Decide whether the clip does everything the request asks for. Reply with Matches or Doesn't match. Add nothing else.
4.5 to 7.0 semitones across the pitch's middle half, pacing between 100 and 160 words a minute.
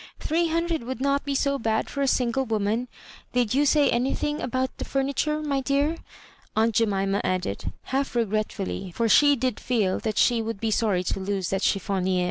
Doesn't match